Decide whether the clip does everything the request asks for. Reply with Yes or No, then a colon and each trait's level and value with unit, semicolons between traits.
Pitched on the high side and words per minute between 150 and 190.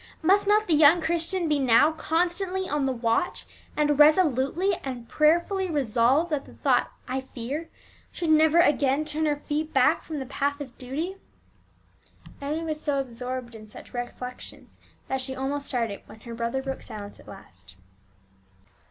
Yes: very high, 285 Hz; average, 160 wpm